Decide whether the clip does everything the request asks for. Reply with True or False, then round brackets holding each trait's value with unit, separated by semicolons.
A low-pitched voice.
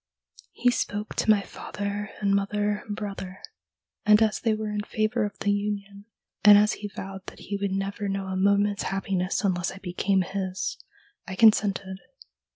False (200 Hz)